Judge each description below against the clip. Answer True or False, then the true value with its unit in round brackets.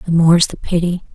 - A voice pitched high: False (170 Hz)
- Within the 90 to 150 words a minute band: False (210 wpm)